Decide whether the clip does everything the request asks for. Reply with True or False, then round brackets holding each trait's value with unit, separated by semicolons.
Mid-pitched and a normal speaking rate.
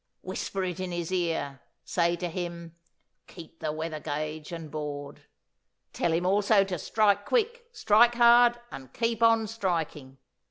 True (175 Hz; 150 wpm)